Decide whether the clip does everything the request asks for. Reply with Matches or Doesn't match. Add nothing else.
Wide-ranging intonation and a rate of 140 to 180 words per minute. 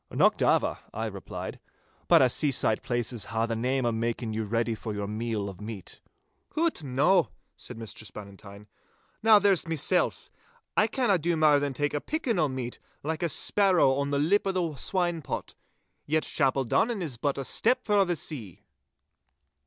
Matches